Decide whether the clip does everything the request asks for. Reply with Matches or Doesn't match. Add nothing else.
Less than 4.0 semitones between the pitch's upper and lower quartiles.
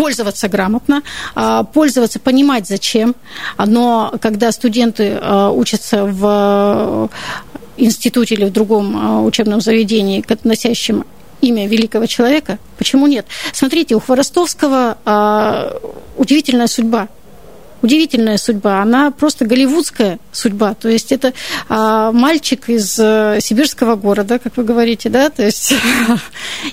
Matches